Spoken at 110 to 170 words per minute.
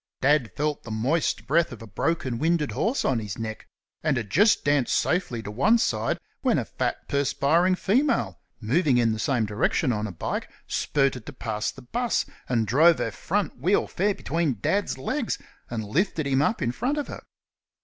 No: average, 190 wpm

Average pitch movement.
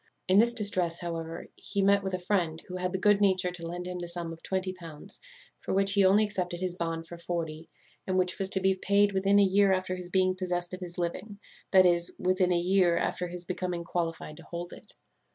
No: narrow, 1.8 semitones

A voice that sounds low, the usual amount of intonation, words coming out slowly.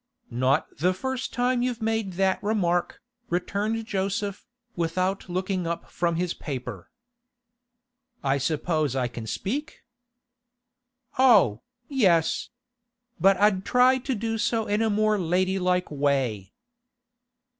No: high, 190 Hz; average, 5.0 semitones; slow, 115 wpm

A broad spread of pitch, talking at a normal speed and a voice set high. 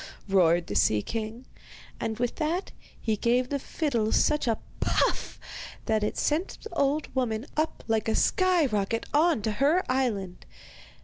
Yes: wide, 5.7 semitones; average, 160 wpm; high, 240 Hz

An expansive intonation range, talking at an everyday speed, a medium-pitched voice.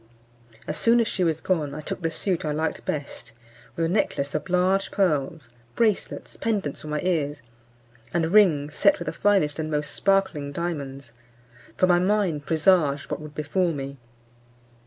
No: average, 4.2 semitones; average, 170 wpm; medium, 160 Hz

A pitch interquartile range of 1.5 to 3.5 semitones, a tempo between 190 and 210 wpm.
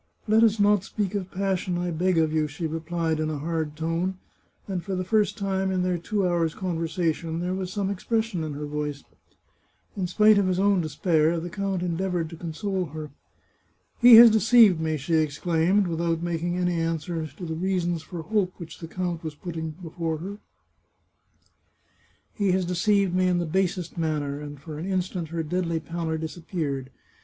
Yes: average, 2.9 semitones; average, 195 wpm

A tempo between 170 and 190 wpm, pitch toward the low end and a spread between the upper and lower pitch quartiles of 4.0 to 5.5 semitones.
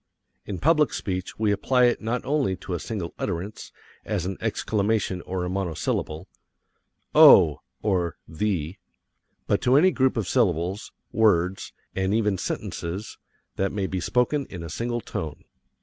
No: average, 150 wpm; low, 100 Hz; average, 4.3 semitones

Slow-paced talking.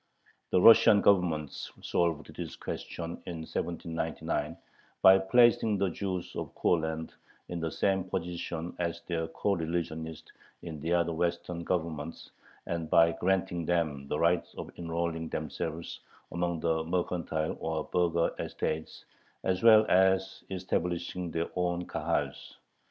Yes: slow, 125 wpm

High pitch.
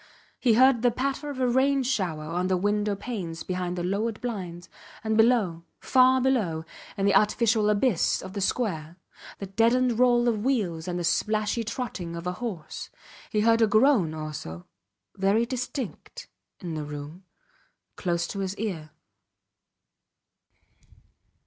Yes: high, 210 Hz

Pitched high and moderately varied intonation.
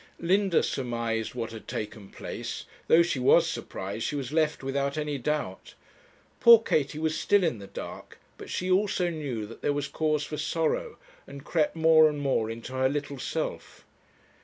No: medium, 145 Hz; average, 4.8 semitones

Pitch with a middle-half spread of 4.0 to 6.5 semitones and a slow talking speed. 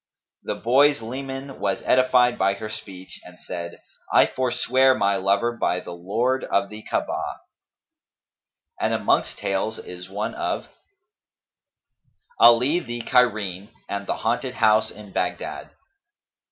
Yes: average, 4.5 semitones; slow, 125 wpm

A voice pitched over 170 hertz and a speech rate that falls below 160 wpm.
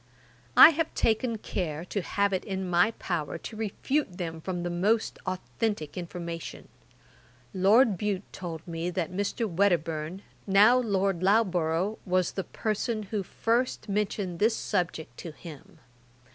Yes: high, 190 Hz; average, 140 wpm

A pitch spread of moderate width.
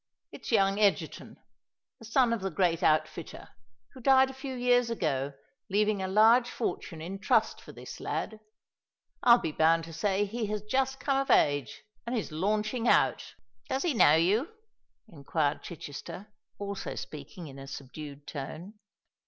No: wide, 6.7 semitones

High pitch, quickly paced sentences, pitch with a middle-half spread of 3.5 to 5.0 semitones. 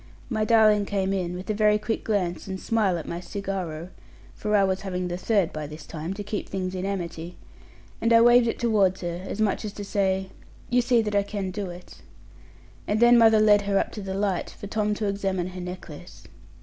No: high, 195 Hz; fast, 220 wpm; narrow, 2.6 semitones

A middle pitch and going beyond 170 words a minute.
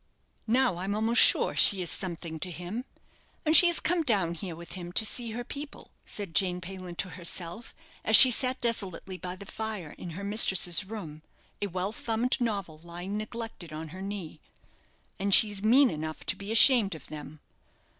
No: high, 195 Hz; average, 185 wpm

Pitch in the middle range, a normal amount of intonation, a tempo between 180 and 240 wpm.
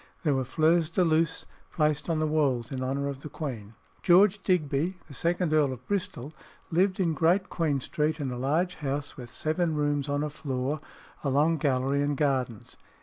Yes: medium, 150 Hz; average, 3.3 semitones; average, 190 wpm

